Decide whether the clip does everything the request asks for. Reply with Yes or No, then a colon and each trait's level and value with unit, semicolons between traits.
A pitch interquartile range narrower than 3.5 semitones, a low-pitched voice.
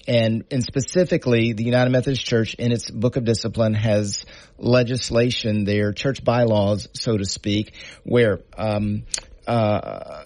Yes: average, 2.8 semitones; low, 115 Hz